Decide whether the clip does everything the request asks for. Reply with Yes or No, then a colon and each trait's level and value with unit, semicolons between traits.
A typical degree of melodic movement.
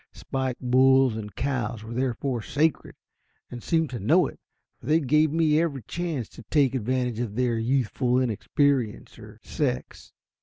Yes: average, 3.1 semitones